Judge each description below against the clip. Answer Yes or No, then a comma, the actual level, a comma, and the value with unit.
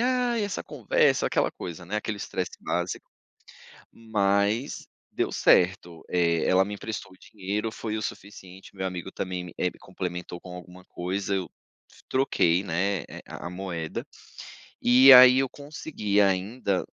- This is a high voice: No, very low, 95 Hz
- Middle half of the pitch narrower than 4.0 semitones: Yes, average, 3.5 semitones